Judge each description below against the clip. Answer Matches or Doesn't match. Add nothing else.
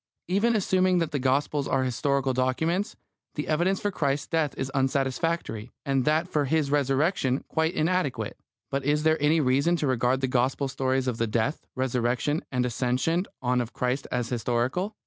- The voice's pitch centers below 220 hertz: Matches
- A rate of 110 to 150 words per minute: Doesn't match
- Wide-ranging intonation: Doesn't match